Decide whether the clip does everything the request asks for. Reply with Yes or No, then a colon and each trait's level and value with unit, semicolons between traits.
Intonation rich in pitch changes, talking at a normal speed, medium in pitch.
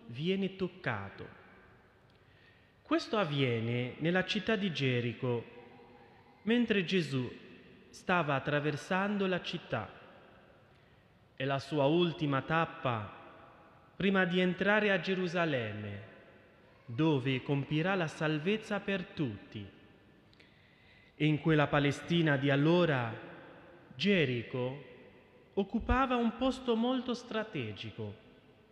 No: wide, 6.8 semitones; slow, 90 wpm; medium, 160 Hz